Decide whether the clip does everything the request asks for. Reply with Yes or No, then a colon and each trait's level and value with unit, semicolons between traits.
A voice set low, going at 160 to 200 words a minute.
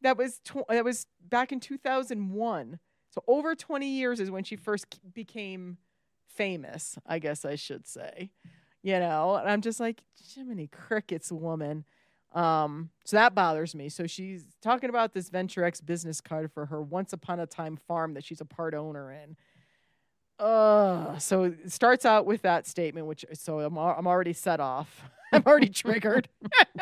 No: medium, 180 Hz; average, 175 wpm